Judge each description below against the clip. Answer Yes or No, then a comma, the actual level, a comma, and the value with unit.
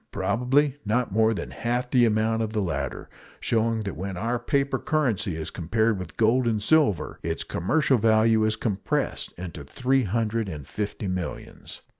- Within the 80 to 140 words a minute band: No, average, 165 wpm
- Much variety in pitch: No, average, 3.7 semitones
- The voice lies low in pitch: Yes, low, 110 Hz